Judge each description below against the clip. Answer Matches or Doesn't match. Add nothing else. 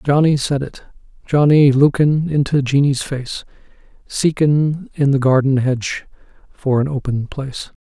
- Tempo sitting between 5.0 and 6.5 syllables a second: Doesn't match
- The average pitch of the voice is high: Doesn't match